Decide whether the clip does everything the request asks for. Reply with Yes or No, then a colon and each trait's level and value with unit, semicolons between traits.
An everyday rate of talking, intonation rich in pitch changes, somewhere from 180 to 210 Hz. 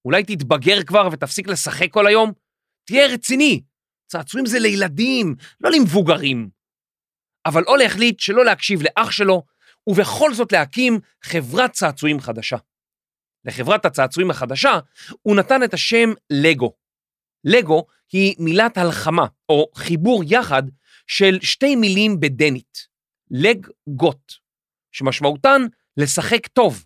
Yes: average, 110 wpm; wide, 7.2 semitones; medium, 185 Hz